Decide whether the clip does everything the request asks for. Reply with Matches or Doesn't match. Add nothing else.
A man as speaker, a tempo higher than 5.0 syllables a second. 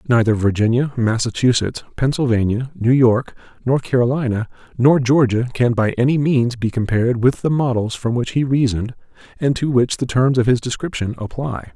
Matches